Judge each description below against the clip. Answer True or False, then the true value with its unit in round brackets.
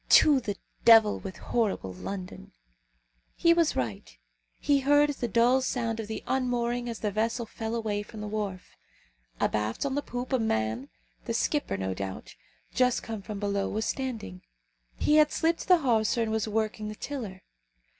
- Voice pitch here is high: True (220 Hz)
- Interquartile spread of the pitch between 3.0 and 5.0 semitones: True (4.0 semitones)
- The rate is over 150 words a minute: True (170 wpm)